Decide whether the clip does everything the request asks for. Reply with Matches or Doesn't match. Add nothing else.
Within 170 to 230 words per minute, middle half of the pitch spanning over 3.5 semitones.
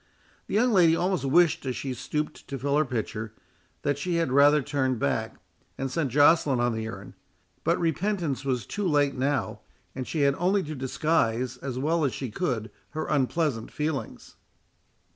Matches